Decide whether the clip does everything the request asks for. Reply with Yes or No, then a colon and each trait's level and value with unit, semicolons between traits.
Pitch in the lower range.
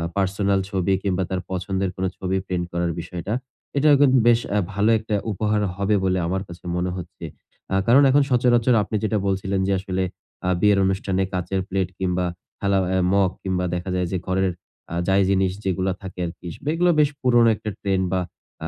Yes: very low, 95 Hz